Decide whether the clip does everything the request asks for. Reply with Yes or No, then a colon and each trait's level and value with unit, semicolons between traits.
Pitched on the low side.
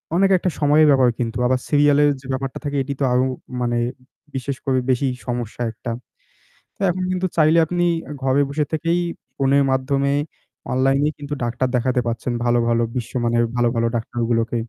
Yes: low, 130 Hz